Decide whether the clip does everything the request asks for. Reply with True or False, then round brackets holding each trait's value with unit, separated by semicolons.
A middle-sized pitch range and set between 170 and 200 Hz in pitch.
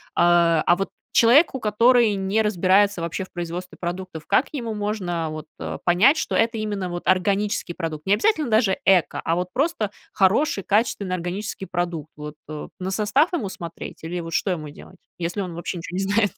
True (3.6 semitones; 190 Hz)